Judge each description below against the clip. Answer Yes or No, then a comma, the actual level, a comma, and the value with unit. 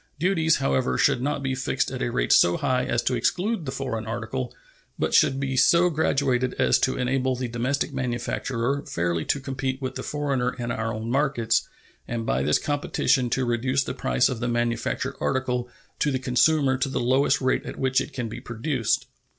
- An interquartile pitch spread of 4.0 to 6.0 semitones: No, narrow, 2.4 semitones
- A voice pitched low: Yes, low, 130 Hz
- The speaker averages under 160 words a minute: No, average, 195 wpm